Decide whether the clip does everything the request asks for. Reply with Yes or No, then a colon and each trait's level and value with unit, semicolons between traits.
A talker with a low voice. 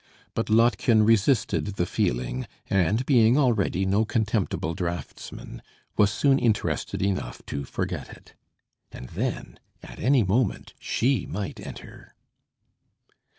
Yes: low, 105 Hz